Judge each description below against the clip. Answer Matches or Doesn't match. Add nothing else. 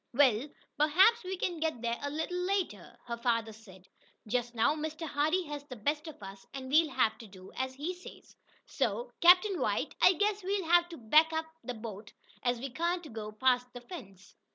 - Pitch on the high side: Matches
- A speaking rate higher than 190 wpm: Matches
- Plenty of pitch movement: Matches